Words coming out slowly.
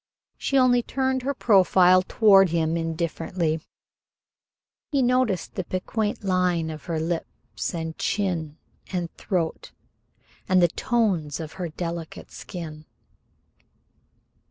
Yes: slow, 115 wpm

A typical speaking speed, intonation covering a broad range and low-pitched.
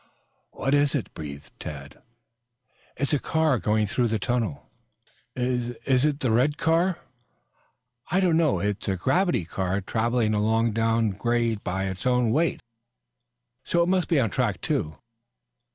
Yes: average, 150 wpm; wide, 5.7 semitones; low, 120 Hz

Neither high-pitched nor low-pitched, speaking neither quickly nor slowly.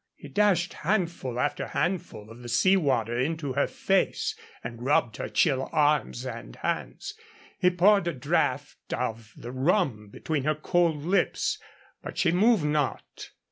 Yes: medium, 150 Hz; average, 150 wpm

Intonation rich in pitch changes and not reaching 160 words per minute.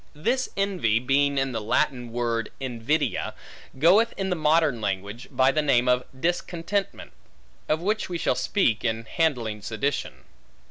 Yes: wide, 6.3 semitones; average, 145 wpm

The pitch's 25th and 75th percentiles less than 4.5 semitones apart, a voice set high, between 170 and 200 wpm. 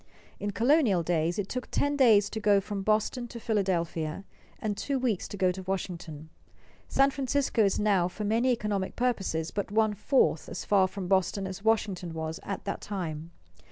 Yes: average, 3.5 semitones; high, 200 Hz; average, 180 wpm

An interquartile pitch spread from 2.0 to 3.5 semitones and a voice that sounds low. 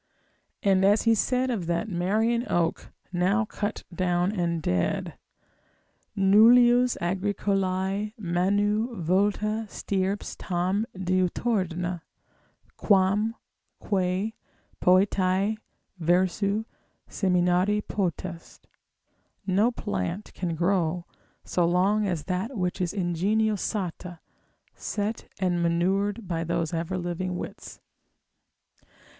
No: average, 2.8 semitones; high, 190 Hz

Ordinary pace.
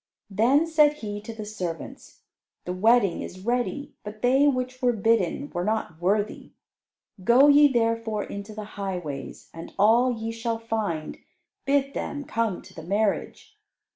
Yes: average, 150 wpm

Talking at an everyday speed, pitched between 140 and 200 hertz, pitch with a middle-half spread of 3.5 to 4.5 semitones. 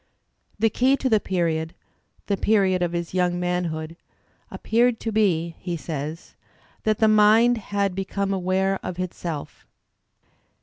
Yes: average, 160 wpm; medium, 185 Hz; average, 3.8 semitones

